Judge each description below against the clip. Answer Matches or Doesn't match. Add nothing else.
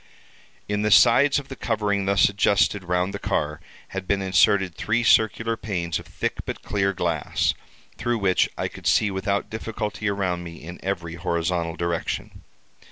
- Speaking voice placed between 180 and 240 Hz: Doesn't match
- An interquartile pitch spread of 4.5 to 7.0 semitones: Doesn't match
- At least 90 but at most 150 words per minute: Doesn't match